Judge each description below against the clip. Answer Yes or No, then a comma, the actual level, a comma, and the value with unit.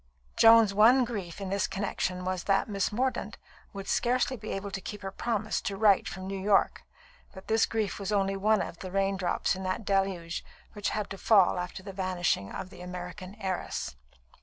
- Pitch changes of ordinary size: No, narrow, 2.2 semitones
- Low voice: No, high, 195 Hz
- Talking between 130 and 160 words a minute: No, average, 195 wpm